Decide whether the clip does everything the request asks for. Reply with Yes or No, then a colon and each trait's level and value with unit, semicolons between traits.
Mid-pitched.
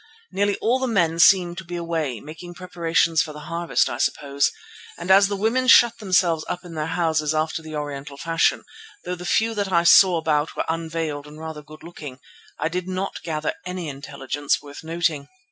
Yes: medium, 165 Hz